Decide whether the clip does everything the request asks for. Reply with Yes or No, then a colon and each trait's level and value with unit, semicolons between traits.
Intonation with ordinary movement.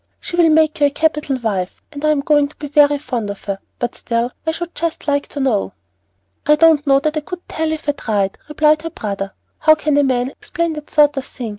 Yes: average, 3.6 semitones